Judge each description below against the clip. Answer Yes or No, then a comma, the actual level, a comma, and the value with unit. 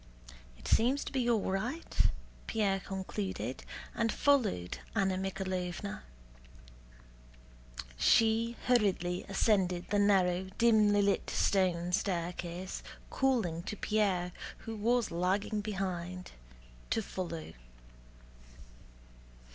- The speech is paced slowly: Yes, slow, 90 wpm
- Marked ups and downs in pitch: No, average, 3.5 semitones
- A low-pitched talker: No, high, 195 Hz